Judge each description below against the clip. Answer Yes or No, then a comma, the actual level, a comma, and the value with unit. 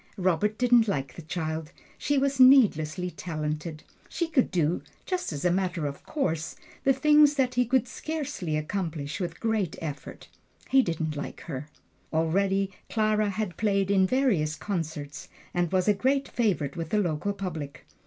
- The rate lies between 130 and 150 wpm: No, average, 160 wpm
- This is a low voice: No, medium, 185 Hz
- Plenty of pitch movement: Yes, wide, 6.8 semitones